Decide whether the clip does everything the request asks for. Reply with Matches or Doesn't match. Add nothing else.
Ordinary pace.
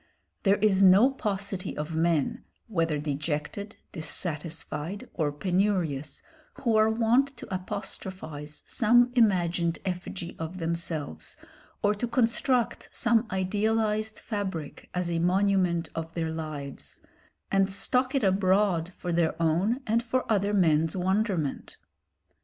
Doesn't match